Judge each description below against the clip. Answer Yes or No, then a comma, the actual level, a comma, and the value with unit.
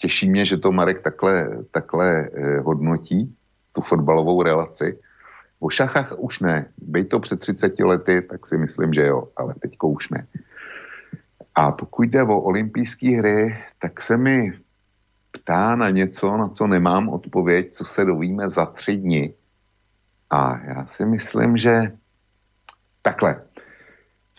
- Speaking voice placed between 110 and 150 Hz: No, low, 100 Hz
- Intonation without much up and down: No, average, 3.2 semitones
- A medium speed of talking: Yes, average, 145 wpm